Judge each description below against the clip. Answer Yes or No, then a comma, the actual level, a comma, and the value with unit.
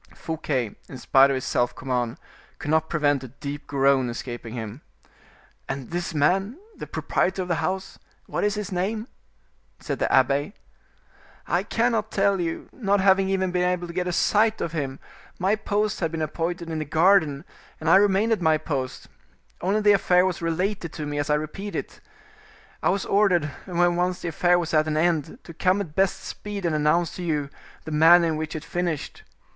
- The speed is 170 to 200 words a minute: Yes, average, 195 wpm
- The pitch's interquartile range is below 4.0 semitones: No, average, 4.4 semitones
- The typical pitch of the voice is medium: Yes, medium, 170 Hz